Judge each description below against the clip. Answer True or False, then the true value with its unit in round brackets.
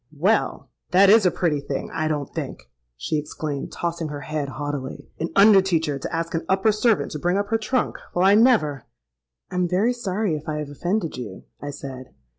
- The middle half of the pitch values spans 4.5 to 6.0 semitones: True (5.1 semitones)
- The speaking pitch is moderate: True (165 Hz)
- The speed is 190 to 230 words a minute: True (195 wpm)